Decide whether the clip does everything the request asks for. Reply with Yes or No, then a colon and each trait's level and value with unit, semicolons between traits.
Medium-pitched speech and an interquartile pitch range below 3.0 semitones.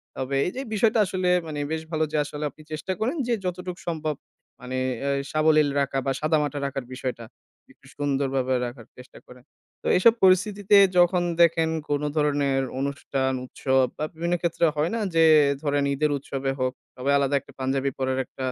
No: medium, 145 Hz; average, 3.8 semitones